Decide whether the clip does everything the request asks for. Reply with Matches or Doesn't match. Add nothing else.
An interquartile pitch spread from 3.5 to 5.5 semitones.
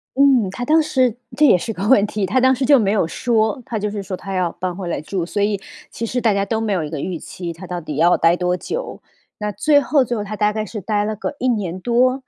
Matches